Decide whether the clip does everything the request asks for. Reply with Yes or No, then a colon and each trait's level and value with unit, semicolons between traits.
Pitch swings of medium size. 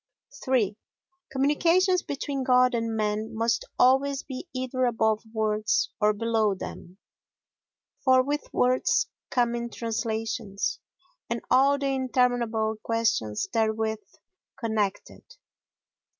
Yes: average, 3.0 semitones